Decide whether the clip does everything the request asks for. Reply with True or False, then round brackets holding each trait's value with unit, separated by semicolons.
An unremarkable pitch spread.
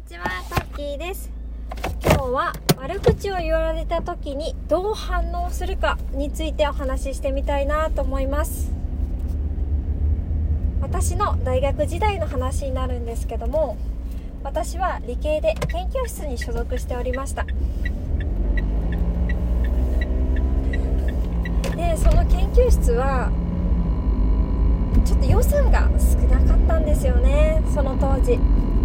True (4.9 semitones)